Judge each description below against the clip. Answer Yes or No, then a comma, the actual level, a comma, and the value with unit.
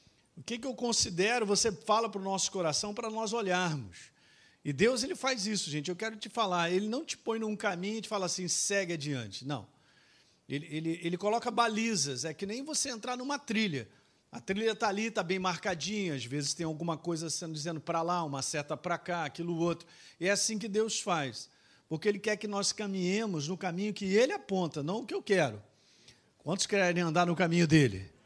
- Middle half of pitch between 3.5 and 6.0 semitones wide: Yes, average, 5.2 semitones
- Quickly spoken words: Yes, fast, 210 wpm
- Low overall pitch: No, medium, 185 Hz